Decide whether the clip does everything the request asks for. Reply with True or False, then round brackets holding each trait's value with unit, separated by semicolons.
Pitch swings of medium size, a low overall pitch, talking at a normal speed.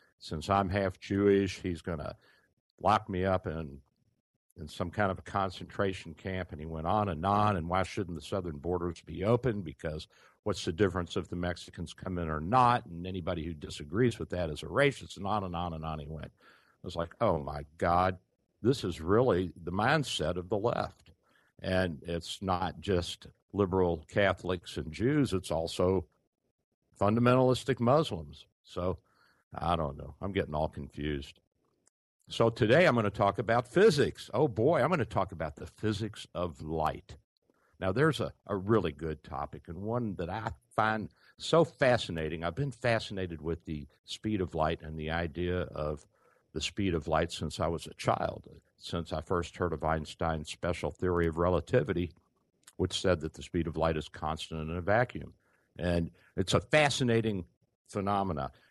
True (4.0 semitones; 90 Hz; 180 wpm)